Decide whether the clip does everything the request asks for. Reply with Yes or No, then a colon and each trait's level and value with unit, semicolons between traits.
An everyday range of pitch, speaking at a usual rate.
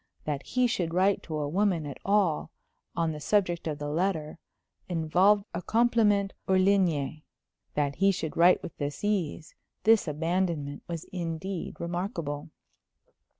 Yes: average, 4.2 semitones; average, 145 wpm